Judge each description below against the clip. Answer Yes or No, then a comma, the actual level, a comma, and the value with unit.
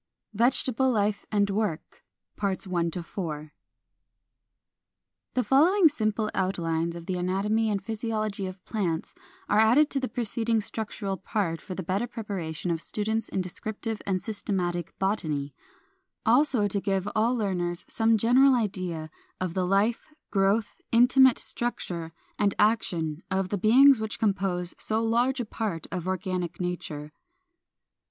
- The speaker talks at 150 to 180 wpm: No, slow, 135 wpm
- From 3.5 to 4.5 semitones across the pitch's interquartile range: Yes, average, 3.9 semitones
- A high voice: Yes, high, 200 Hz